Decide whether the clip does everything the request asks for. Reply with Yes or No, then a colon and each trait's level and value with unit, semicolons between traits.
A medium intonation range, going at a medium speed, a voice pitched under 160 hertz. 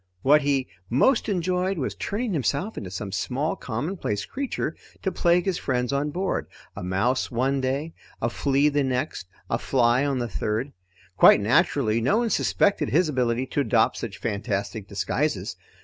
No: wide, 5.9 semitones; average, 165 wpm; low, 135 Hz